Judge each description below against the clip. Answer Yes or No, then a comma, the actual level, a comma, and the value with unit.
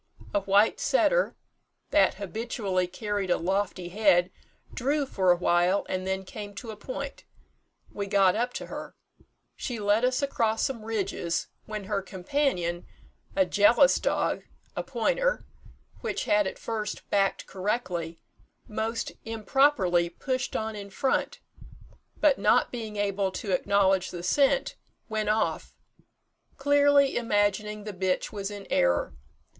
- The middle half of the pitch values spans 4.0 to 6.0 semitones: No, average, 3.6 semitones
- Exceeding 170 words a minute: No, slow, 135 wpm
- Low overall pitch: No, high, 205 Hz